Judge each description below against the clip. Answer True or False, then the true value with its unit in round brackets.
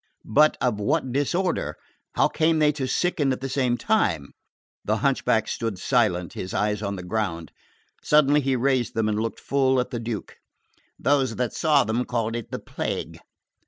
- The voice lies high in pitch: False (125 Hz)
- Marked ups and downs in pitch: False (4.7 semitones)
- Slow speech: False (175 wpm)